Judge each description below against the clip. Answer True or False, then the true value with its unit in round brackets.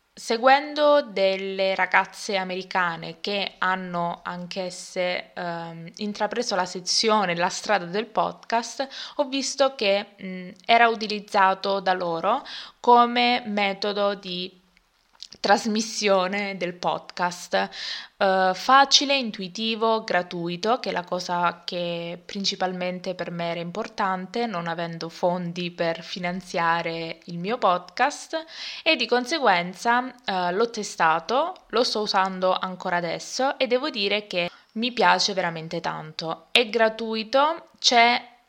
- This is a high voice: True (195 Hz)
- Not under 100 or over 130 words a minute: True (115 wpm)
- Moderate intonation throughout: True (4.4 semitones)